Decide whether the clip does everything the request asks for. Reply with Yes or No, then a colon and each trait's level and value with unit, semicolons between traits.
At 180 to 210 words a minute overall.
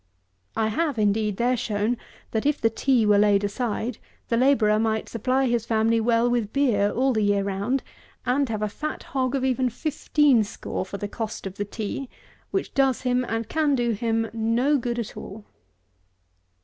Yes: average, 185 wpm